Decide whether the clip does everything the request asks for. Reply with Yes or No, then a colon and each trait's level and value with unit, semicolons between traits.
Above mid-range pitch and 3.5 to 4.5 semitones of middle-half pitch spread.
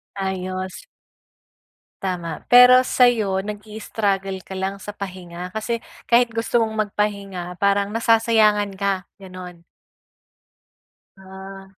No: high, 200 Hz; narrow, 2.5 semitones